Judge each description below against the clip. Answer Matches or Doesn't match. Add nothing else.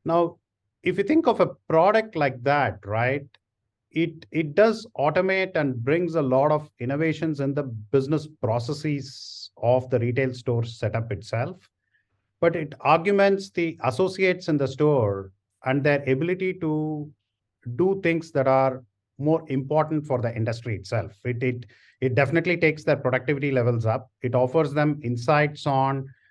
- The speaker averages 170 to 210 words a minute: Doesn't match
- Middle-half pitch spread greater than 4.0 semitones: Matches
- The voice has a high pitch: Doesn't match